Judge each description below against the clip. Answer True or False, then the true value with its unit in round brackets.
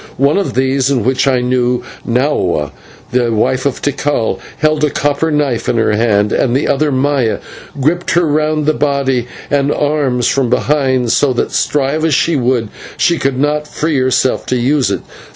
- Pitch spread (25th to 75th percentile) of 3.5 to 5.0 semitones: False (3.0 semitones)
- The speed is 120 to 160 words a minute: False (180 wpm)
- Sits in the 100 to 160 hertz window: True (135 Hz)